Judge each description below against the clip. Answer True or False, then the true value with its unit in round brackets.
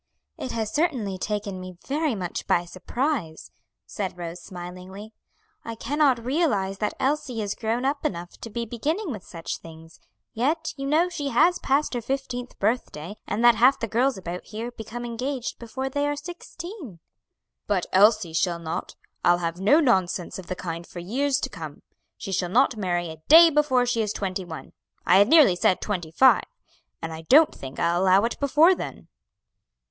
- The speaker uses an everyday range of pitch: False (7.2 semitones)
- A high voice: True (220 Hz)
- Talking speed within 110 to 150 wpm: False (180 wpm)